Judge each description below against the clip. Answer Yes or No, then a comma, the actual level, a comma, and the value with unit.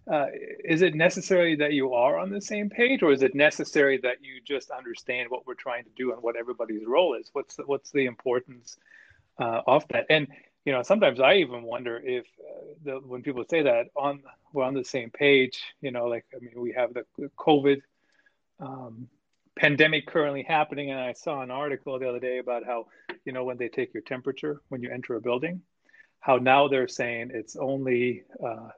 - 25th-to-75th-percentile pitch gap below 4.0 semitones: Yes, average, 3.2 semitones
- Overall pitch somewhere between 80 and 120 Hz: No, low, 135 Hz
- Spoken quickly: Yes, fast, 215 wpm